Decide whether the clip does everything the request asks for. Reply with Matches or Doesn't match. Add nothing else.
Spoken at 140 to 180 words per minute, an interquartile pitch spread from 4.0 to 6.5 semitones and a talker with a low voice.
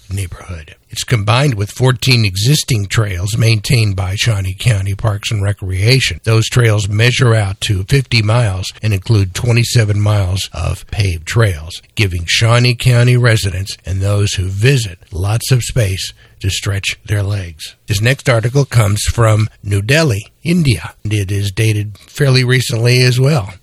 Doesn't match